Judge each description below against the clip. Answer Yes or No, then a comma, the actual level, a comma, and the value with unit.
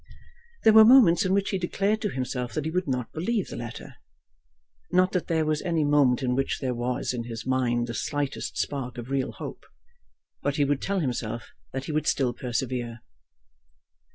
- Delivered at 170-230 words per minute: Yes, average, 190 wpm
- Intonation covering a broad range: Yes, wide, 5.9 semitones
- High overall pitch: No, low, 135 Hz